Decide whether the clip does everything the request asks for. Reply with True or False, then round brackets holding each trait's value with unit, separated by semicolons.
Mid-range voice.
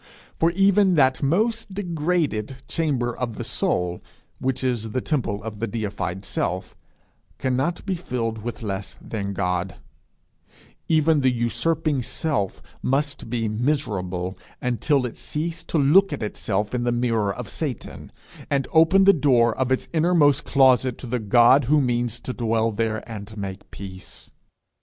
False (125 Hz)